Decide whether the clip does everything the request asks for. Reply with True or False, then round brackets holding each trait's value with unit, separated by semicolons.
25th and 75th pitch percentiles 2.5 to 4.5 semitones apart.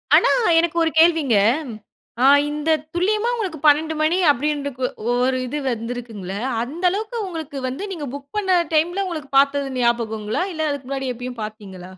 False (5.1 semitones)